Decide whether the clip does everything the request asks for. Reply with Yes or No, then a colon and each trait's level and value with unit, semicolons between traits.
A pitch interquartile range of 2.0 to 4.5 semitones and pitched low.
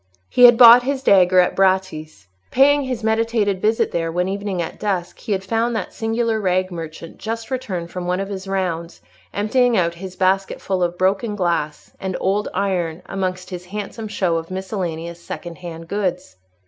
No: average, 3.5 semitones; high, 190 Hz